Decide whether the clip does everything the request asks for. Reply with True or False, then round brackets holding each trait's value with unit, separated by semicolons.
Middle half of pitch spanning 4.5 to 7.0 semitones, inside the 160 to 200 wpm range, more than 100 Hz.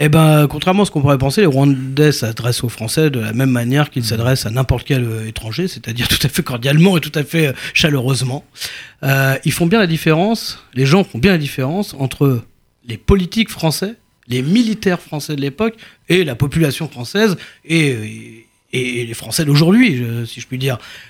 True (5.1 semitones; 195 wpm; 140 Hz)